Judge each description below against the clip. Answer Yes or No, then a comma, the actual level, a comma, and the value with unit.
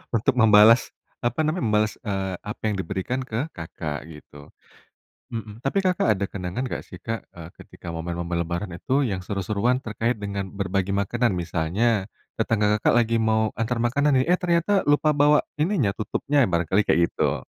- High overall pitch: No, low, 105 Hz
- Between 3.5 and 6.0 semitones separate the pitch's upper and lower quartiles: Yes, average, 4.8 semitones